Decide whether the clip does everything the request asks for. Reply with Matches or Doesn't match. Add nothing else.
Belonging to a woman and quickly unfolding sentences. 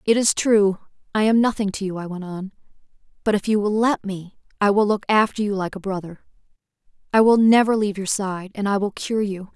Matches